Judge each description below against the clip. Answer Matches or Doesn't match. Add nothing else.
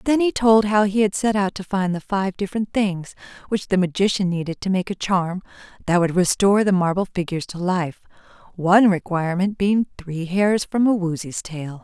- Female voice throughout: Matches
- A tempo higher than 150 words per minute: Matches